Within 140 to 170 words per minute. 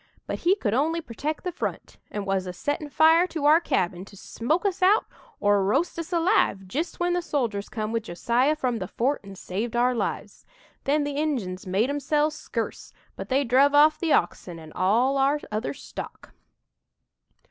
No: average, 185 wpm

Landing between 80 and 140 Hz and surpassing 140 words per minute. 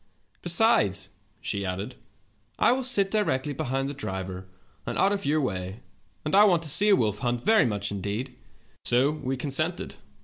Yes: low, 135 Hz; average, 170 wpm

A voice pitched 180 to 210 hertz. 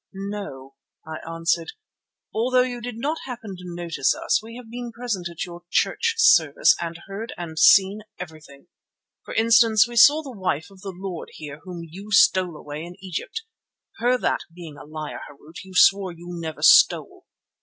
Yes: medium, 185 Hz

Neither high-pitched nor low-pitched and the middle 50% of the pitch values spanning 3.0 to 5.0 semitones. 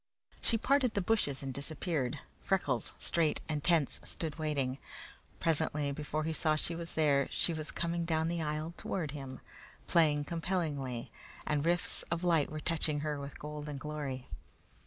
No: medium, 155 Hz; narrow, 2.6 semitones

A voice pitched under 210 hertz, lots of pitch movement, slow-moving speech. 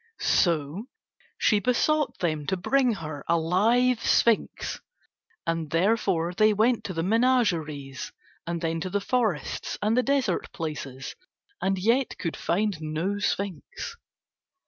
Yes: high, 190 Hz; wide, 5.7 semitones; slow, 130 wpm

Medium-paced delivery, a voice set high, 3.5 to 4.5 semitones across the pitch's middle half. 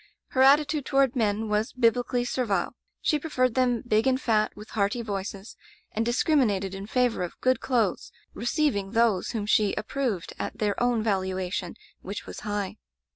Yes: average, 170 wpm; high, 225 Hz; average, 3.8 semitones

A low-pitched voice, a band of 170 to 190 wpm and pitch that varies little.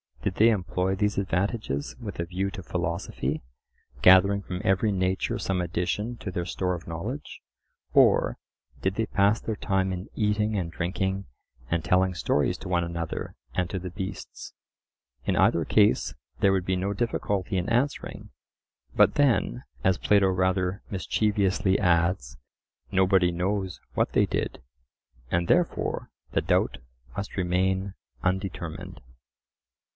No: very low, 95 Hz; average, 140 wpm; narrow, 2.1 semitones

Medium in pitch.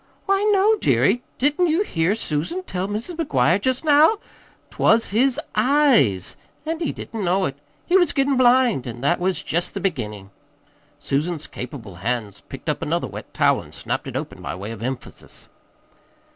No: high, 200 Hz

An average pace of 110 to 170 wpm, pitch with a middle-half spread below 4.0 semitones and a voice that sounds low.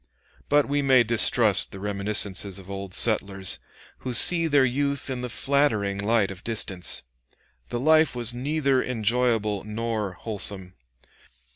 No: slow, 135 wpm; average, 4.8 semitones; low, 115 Hz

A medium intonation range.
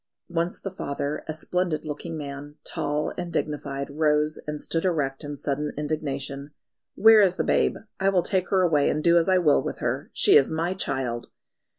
Yes: average, 3.4 semitones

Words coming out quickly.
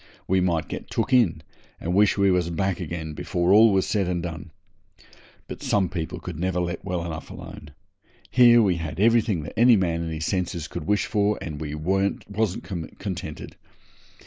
No: average, 175 wpm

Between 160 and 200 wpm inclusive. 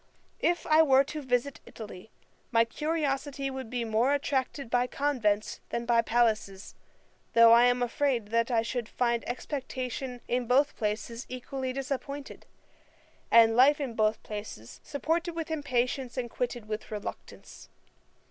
No: average, 140 wpm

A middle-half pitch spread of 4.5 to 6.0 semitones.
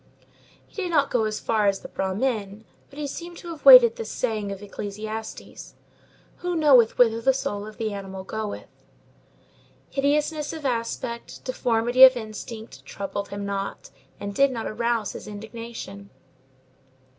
Yes: average, 5.0 semitones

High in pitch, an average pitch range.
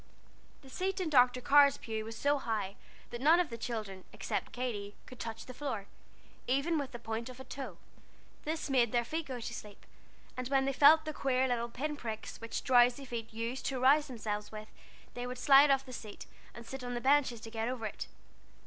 Yes: very high, 250 Hz; average, 3.3 semitones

